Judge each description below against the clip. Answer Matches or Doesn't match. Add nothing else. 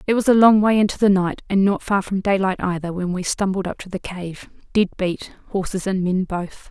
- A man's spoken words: Doesn't match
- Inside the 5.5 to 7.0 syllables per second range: Doesn't match